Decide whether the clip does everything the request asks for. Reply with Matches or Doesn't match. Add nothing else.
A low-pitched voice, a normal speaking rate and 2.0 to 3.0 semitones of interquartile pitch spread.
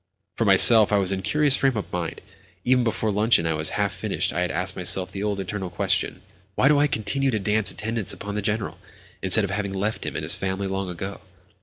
Doesn't match